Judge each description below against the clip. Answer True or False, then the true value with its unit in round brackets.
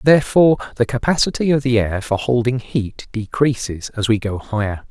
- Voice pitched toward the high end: False (120 Hz)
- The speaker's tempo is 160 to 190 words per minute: True (170 wpm)